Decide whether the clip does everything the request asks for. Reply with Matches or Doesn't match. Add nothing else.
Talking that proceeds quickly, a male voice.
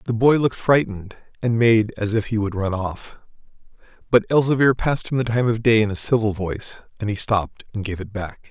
Matches